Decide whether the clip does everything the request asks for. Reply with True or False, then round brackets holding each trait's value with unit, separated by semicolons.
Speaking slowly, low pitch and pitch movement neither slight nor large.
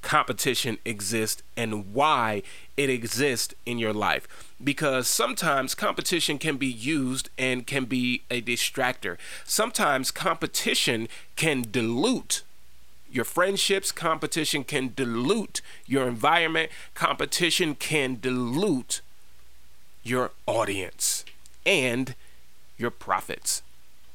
True (95 wpm; 125 Hz; 4.8 semitones)